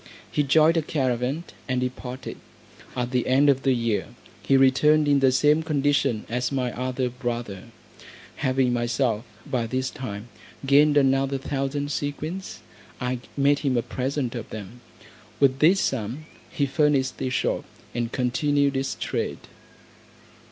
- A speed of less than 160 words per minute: Yes, average, 145 wpm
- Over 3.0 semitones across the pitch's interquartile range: No, narrow, 2.5 semitones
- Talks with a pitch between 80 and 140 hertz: Yes, low, 135 Hz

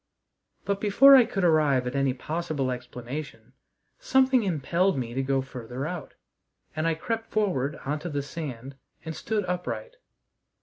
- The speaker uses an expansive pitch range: Yes, wide, 6.6 semitones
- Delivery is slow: No, average, 150 wpm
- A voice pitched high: No, medium, 155 Hz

